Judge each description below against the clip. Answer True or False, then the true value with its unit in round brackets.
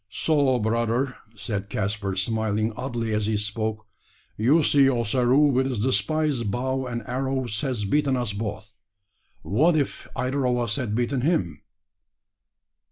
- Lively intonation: False (3.8 semitones)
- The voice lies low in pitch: True (120 Hz)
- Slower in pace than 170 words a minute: True (140 wpm)